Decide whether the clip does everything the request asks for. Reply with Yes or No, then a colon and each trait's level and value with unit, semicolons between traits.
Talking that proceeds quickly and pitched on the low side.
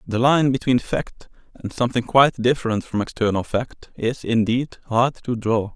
No: average, 165 wpm; low, 120 Hz